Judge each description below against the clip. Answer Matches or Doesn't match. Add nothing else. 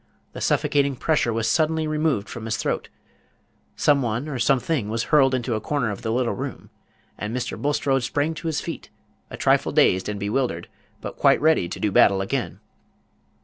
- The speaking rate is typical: Matches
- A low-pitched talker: Matches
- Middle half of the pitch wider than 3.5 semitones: Matches